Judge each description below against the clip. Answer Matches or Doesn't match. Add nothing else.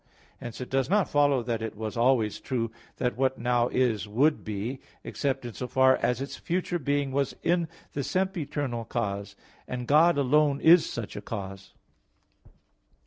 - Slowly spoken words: Doesn't match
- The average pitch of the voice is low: Matches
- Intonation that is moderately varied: Matches